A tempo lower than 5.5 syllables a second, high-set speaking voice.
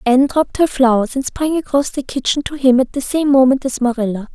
No: 5.9 syllables/s; very high, 265 Hz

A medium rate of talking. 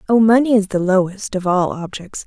No: fast, 210 wpm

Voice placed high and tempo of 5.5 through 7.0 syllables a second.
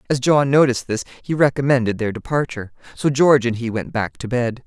No: low, 125 Hz; 6.0 syllables/s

